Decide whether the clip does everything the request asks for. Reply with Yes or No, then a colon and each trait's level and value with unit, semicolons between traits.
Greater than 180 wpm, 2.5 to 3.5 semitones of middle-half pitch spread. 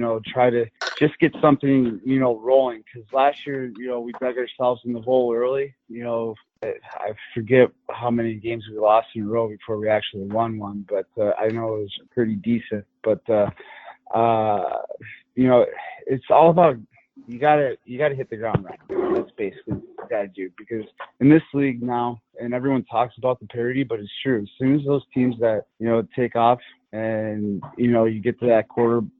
Yes: average, 200 wpm; average, 2.9 semitones